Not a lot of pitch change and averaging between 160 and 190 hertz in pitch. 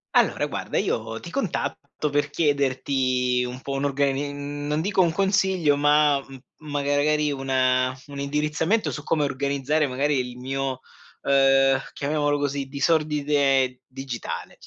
No: narrow, 1.9 semitones; medium, 140 Hz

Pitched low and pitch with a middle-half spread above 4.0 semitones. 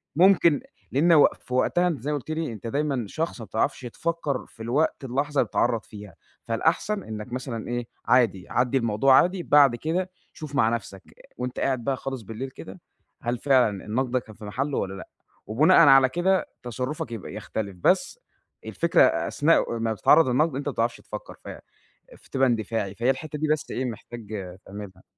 Yes: low, 125 Hz; average, 4.7 semitones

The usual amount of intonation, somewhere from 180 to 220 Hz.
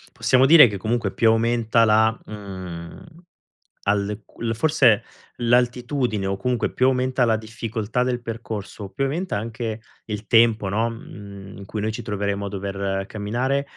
No: average, 3.2 semitones; low, 110 Hz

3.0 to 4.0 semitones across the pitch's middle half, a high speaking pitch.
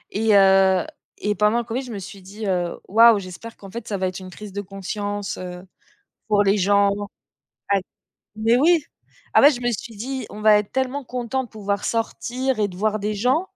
Yes: average, 3.3 semitones; high, 210 Hz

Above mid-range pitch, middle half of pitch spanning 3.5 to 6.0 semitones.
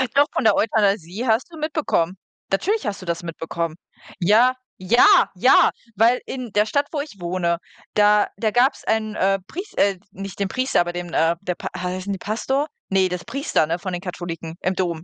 Yes: high, 195 Hz; average, 5.1 semitones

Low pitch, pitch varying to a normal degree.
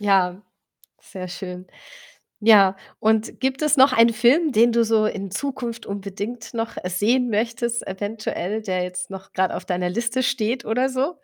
No: high, 220 Hz; average, 3.8 semitones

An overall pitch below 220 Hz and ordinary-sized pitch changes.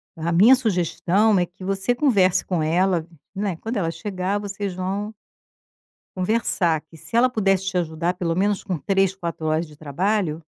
Yes: medium, 185 Hz; average, 3.3 semitones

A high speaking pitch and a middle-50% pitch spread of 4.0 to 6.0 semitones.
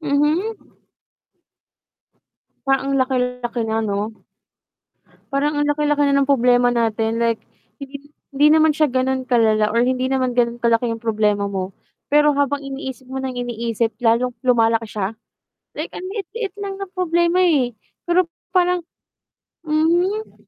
Yes: very high, 260 Hz; average, 4.4 semitones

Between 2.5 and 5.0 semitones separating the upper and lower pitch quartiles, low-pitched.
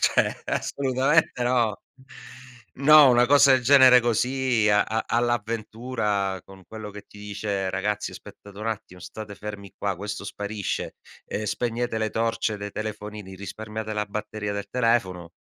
Yes: average, 2.9 semitones; low, 110 Hz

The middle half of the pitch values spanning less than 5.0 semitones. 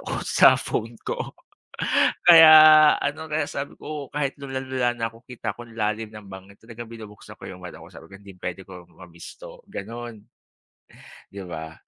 No: wide, 5.5 semitones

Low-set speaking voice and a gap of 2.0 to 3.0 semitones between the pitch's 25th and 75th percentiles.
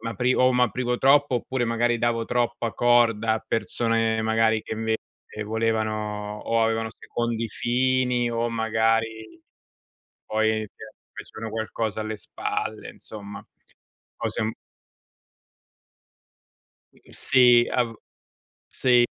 No: low, 115 Hz; narrow, 1.5 semitones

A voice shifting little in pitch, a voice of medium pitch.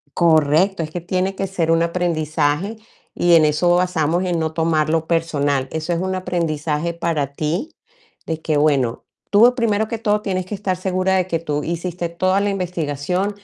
No: average, 3.1 semitones; medium, 170 Hz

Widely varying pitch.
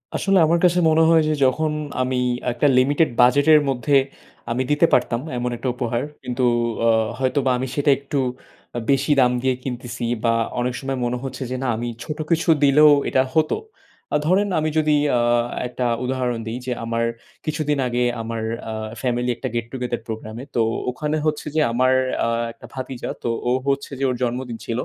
No: average, 3.3 semitones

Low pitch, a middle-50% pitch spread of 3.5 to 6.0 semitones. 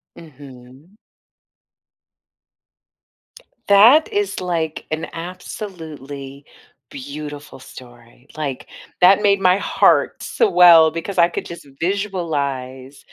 No: medium, 160 Hz; average, 5.1 semitones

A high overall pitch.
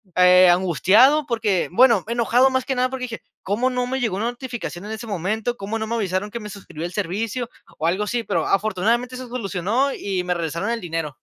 Yes: high, 220 Hz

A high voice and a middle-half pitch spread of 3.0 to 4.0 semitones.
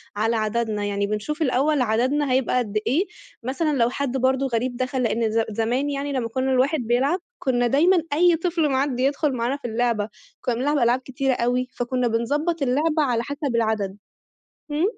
Yes: very high, 255 Hz; average, 3.5 semitones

